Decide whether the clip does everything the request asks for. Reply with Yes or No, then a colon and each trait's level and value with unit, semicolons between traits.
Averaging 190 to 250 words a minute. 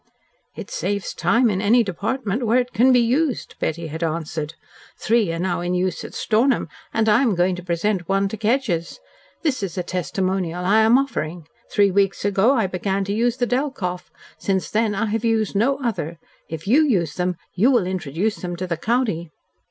Yes: average, 195 wpm